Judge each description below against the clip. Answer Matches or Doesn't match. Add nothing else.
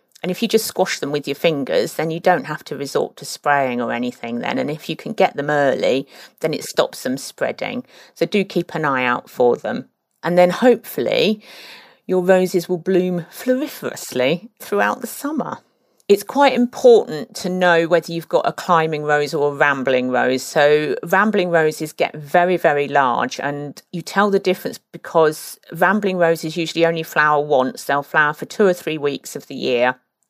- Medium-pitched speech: Matches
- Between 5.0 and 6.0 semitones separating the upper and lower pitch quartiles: Doesn't match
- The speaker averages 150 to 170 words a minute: Doesn't match